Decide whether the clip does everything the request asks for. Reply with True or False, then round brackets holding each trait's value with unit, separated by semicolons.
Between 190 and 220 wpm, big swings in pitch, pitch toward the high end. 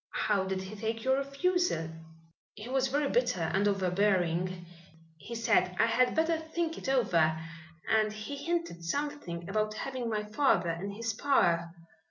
False (155 wpm; 6.6 semitones; 215 Hz)